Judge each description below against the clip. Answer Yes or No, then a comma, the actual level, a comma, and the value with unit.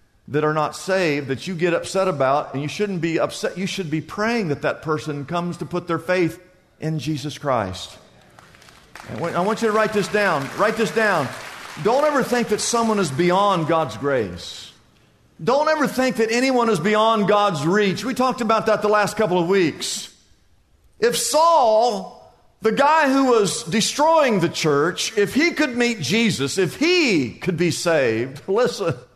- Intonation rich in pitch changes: Yes, wide, 5.9 semitones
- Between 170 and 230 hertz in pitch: Yes, high, 190 Hz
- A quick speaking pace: No, average, 180 wpm